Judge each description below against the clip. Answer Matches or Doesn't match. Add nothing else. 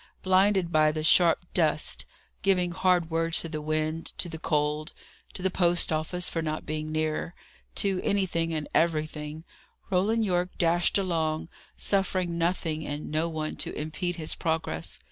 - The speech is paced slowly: Doesn't match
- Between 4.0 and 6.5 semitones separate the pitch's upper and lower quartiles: Doesn't match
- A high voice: Doesn't match